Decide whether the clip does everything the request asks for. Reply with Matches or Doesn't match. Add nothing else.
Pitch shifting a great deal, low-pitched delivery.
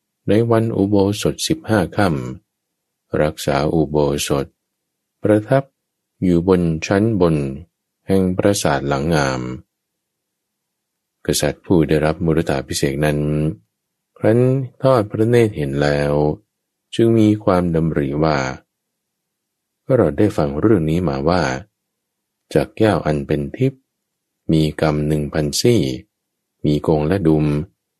Matches